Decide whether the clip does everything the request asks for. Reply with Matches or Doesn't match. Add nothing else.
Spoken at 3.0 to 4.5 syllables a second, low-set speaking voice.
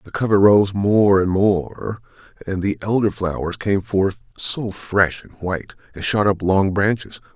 Matches